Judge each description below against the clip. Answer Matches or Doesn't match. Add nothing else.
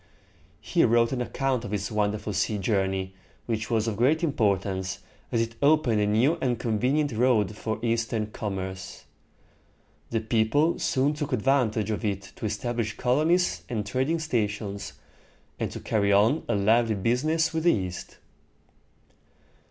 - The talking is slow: Doesn't match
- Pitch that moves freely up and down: Doesn't match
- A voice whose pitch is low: Matches